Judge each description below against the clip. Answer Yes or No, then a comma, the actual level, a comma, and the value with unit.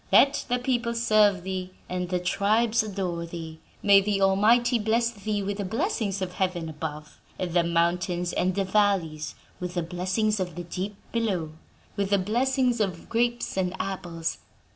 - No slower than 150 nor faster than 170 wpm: Yes, average, 165 wpm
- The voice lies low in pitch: No, high, 195 Hz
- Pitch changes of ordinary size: Yes, average, 3.6 semitones